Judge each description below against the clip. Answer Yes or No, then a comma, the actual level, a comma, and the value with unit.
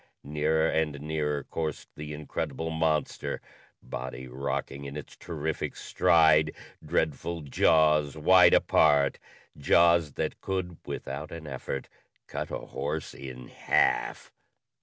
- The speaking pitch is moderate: No, very low, 75 Hz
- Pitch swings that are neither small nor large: No, narrow, 2.2 semitones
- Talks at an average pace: No, slow, 115 wpm